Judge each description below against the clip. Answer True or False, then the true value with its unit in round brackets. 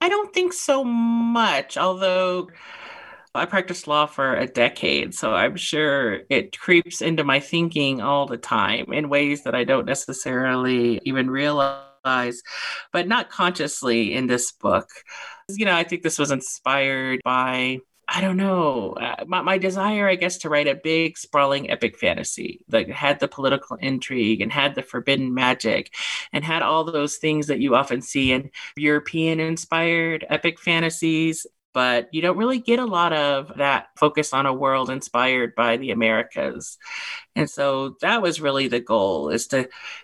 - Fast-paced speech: False (165 wpm)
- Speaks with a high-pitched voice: False (150 Hz)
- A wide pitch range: False (5.0 semitones)